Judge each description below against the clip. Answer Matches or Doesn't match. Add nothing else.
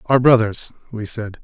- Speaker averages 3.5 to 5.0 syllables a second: Matches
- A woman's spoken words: Doesn't match